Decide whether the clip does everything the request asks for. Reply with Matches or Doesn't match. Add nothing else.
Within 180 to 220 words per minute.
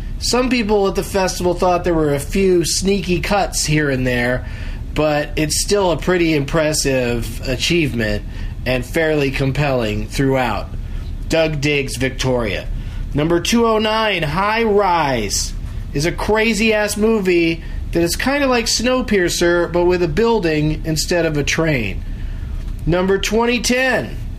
Doesn't match